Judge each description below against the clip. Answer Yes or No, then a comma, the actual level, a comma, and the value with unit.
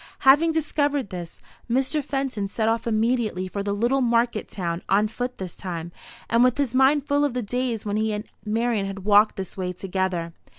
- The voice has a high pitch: Yes, high, 225 Hz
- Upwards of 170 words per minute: Yes, average, 195 wpm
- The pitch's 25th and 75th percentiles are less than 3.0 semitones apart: No, average, 4.6 semitones